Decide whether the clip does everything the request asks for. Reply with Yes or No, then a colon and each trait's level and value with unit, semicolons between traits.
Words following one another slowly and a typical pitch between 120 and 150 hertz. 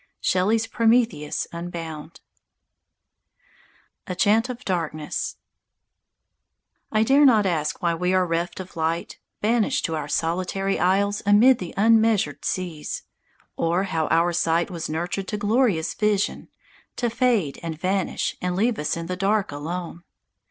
No: slow, 125 wpm; medium, 185 Hz